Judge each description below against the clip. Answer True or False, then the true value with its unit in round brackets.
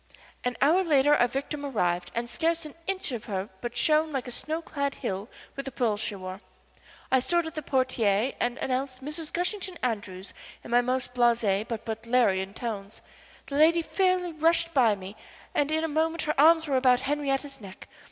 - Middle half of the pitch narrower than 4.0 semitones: False (5.4 semitones)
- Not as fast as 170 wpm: False (190 wpm)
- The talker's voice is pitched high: True (265 Hz)